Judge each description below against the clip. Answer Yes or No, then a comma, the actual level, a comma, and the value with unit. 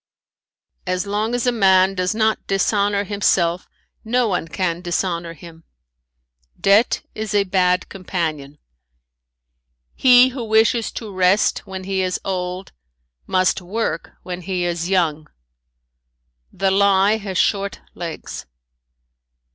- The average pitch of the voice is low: No, high, 190 Hz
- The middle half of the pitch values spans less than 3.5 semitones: Yes, narrow, 2.5 semitones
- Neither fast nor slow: No, slow, 120 wpm